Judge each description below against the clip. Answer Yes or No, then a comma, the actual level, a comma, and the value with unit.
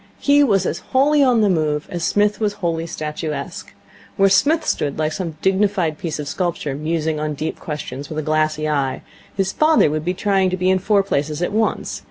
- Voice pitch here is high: No, medium, 170 Hz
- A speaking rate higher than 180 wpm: Yes, fast, 205 wpm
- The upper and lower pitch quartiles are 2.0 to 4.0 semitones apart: No, average, 4.7 semitones